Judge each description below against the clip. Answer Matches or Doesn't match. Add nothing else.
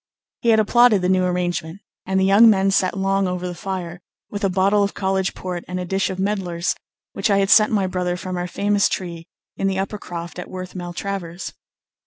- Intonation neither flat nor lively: Doesn't match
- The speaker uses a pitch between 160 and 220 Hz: Matches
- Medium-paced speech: Doesn't match